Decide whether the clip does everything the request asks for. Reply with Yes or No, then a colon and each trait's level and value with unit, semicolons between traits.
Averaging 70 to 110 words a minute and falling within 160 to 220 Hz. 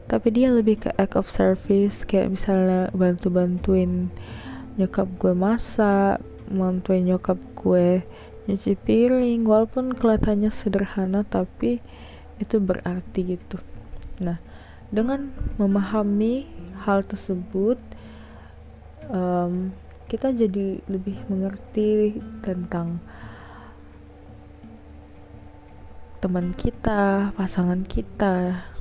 Yes: slow, 85 wpm; high, 190 Hz